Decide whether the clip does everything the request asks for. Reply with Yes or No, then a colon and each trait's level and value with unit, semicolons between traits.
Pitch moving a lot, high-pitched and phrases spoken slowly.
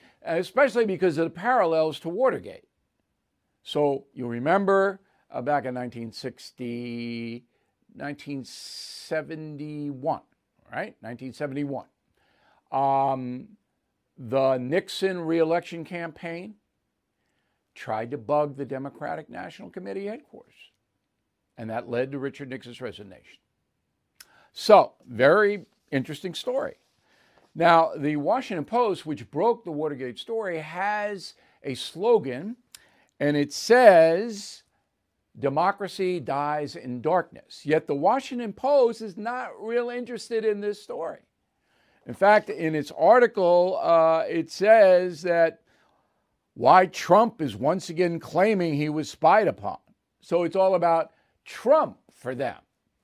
No: wide, 6.2 semitones; medium, 165 Hz; slow, 110 wpm